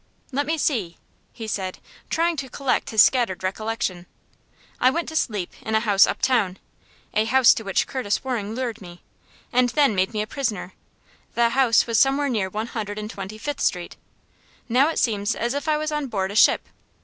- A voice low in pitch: No, high, 230 Hz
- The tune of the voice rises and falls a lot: No, average, 4.5 semitones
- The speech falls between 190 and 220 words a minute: Yes, average, 195 wpm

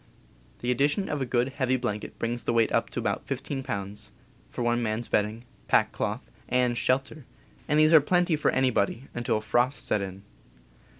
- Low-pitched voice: Yes, low, 125 Hz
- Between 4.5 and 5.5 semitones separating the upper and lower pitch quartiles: No, average, 3.1 semitones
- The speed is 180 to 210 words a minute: Yes, average, 185 wpm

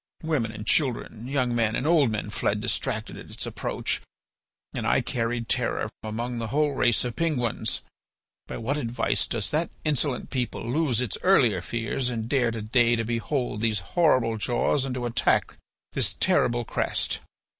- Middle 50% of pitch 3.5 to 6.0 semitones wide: No, average, 3.1 semitones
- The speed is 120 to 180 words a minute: Yes, average, 165 wpm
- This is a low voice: Yes, low, 120 Hz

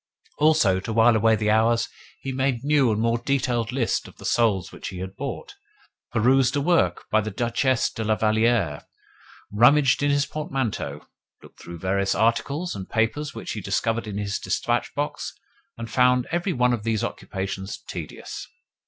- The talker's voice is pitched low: Yes, low, 115 Hz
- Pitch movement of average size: Yes, average, 3.9 semitones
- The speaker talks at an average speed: Yes, average, 170 wpm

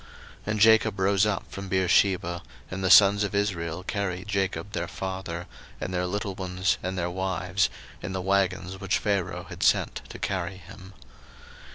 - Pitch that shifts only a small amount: Yes, narrow, 1.5 semitones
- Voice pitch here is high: No, very low, 95 Hz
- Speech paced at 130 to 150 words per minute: No, average, 170 wpm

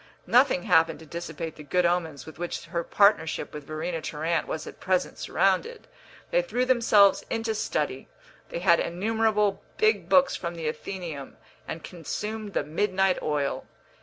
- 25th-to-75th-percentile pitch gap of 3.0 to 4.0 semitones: No, average, 4.7 semitones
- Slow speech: No, average, 155 wpm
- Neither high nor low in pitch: Yes, medium, 175 Hz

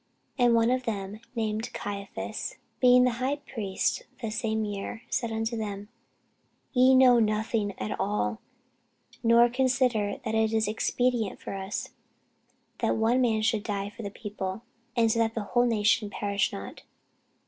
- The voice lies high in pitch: Yes, high, 220 Hz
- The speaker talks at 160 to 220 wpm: No, average, 150 wpm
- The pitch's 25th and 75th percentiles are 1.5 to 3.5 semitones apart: Yes, average, 2.8 semitones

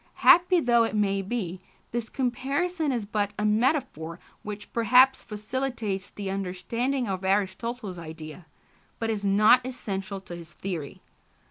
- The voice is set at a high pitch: Yes, high, 210 Hz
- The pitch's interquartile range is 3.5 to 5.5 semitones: Yes, average, 4.4 semitones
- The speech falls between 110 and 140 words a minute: Yes, slow, 135 wpm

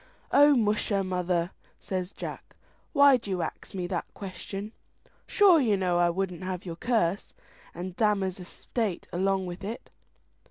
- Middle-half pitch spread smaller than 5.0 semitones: Yes, average, 3.0 semitones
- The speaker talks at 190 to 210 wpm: No, average, 150 wpm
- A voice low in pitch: No, high, 190 Hz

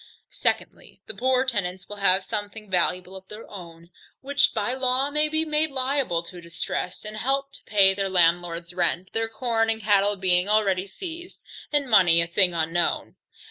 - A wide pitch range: Yes, wide, 6.2 semitones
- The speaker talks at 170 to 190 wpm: Yes, average, 180 wpm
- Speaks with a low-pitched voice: No, high, 205 Hz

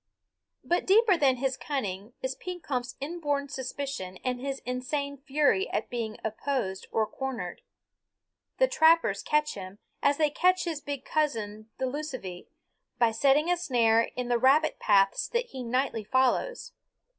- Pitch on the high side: Yes, very high, 265 Hz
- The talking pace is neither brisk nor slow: Yes, average, 145 wpm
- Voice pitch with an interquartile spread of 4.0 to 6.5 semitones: Yes, average, 4.4 semitones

